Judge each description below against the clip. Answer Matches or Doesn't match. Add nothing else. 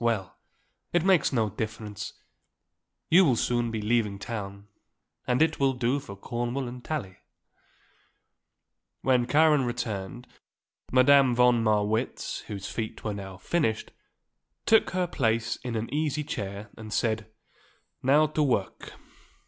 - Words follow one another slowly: Matches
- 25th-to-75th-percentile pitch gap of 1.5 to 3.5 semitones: Doesn't match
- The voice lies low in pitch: Matches